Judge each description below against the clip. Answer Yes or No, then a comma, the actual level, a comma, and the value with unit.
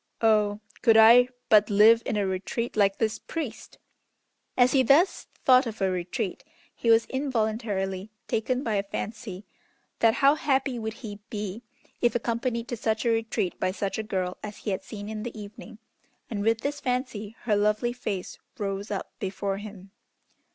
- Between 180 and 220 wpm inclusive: No, average, 170 wpm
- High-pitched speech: Yes, high, 220 Hz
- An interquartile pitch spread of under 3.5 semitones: Yes, average, 2.8 semitones